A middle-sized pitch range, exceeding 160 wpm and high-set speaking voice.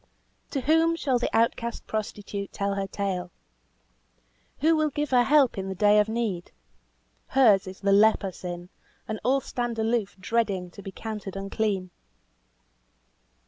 No: average, 3.8 semitones; average, 145 wpm; high, 215 Hz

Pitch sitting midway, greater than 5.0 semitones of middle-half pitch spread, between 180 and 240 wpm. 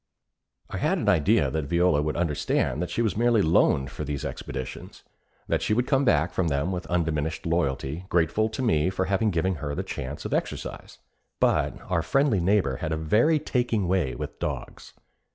No: very low, 85 Hz; wide, 5.6 semitones; average, 190 wpm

